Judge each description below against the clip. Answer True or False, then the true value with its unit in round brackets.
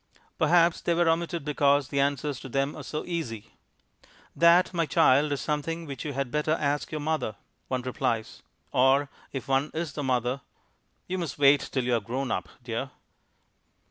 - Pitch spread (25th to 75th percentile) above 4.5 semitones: False (3.3 semitones)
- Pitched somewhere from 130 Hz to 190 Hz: True (140 Hz)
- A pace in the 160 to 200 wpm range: True (175 wpm)